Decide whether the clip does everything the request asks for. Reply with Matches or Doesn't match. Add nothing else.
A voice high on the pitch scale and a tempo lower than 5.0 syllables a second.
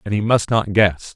Doesn't match